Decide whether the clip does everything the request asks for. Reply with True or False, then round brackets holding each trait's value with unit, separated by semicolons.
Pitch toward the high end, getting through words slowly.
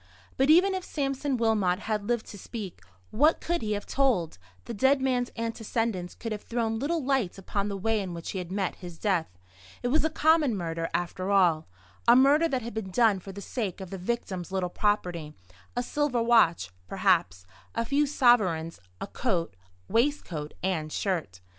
False (215 Hz; 185 wpm)